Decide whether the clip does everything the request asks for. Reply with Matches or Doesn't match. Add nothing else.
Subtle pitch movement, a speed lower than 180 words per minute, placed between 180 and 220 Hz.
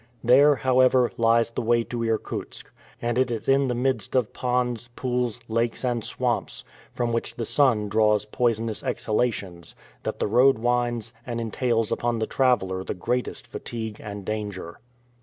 Doesn't match